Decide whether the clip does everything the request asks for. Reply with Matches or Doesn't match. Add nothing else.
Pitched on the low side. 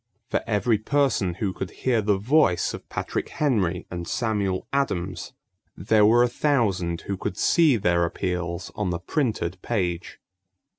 Matches